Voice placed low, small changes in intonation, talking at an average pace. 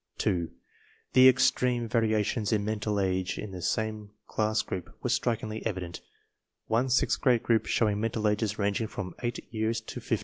Yes: low, 110 Hz; narrow, 1.9 semitones; average, 165 wpm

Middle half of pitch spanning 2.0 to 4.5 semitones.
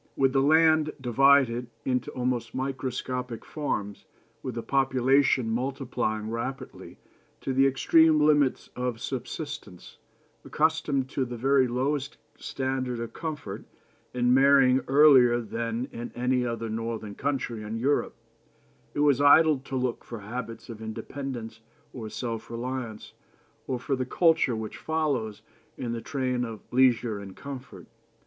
Yes: average, 2.8 semitones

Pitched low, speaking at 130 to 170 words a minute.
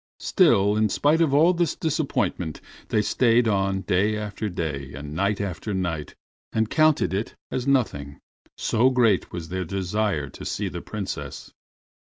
Yes: low, 105 Hz; average, 155 wpm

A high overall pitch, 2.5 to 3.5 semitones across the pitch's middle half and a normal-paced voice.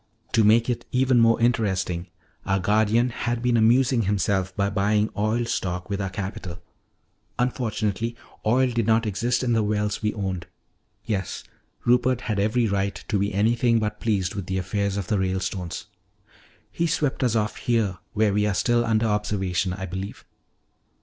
No: low, 105 Hz; average, 3.1 semitones; average, 165 wpm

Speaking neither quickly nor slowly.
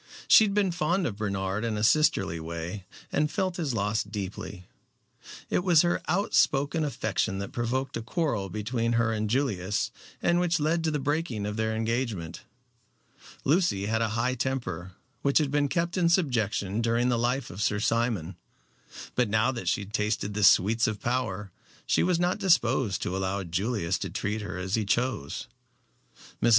Yes: average, 175 wpm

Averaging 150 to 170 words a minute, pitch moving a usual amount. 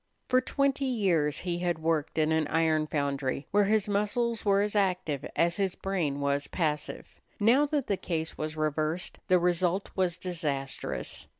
Yes: average, 165 wpm; average, 4.7 semitones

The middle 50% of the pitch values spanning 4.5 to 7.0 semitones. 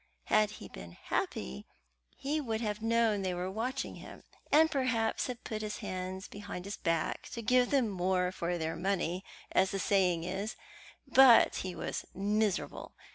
No: average, 3.9 semitones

